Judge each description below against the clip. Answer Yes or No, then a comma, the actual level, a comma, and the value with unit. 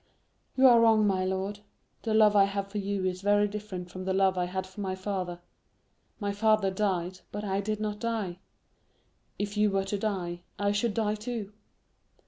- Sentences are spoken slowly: No, average, 190 wpm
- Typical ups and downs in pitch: No, narrow, 2.0 semitones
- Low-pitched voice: No, high, 200 Hz